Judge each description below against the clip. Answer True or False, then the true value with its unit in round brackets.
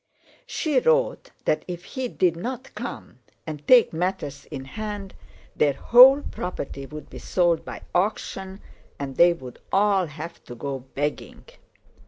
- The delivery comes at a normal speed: True (145 wpm)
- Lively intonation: True (6.4 semitones)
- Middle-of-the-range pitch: True (175 Hz)